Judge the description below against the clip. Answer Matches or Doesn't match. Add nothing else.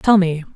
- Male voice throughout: Doesn't match